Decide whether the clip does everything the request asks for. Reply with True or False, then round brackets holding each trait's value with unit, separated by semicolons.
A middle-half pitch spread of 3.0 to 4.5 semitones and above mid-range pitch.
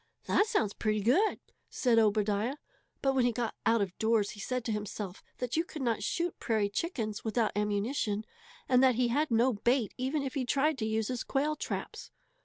True (3.9 semitones; 235 Hz)